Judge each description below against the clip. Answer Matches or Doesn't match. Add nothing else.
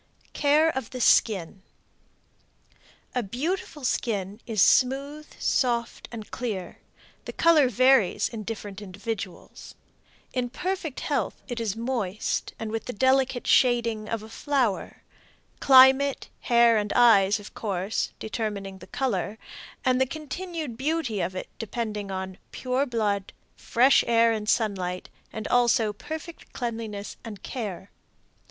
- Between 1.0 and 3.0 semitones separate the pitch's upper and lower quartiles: Doesn't match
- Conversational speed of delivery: Doesn't match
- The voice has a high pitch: Matches